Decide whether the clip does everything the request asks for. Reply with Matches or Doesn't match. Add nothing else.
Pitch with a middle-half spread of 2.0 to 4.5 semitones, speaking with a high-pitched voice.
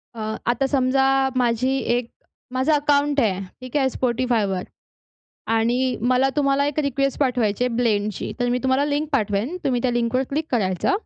Matches